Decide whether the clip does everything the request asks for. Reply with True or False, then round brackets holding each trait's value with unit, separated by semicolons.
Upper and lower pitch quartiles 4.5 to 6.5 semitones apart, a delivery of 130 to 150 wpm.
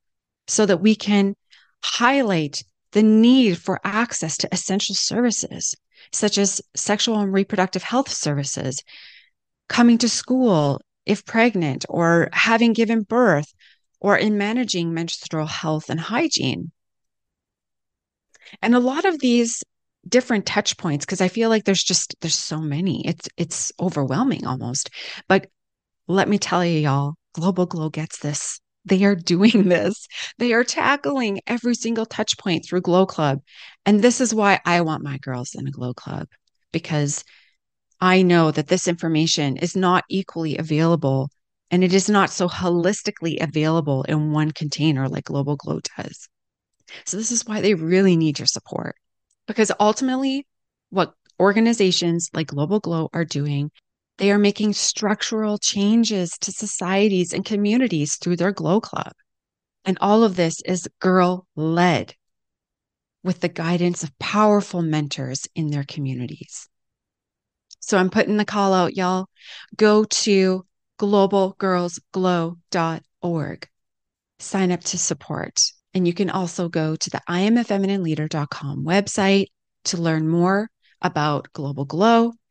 True (4.8 semitones; 140 wpm)